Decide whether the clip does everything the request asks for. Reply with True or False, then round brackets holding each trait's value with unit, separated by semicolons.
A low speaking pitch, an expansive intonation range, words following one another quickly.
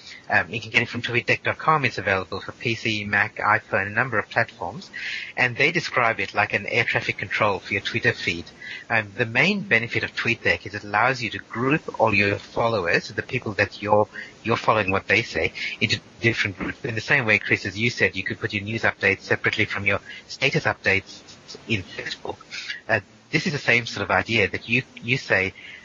False (110 Hz; 2.7 semitones; 210 wpm)